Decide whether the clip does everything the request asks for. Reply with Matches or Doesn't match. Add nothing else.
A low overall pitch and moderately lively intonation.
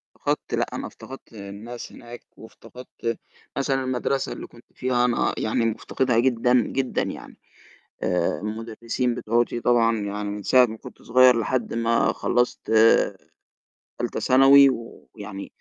Doesn't match